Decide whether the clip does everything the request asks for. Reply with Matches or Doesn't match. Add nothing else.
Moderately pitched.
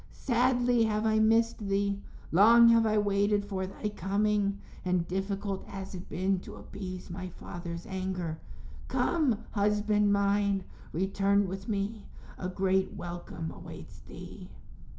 Doesn't match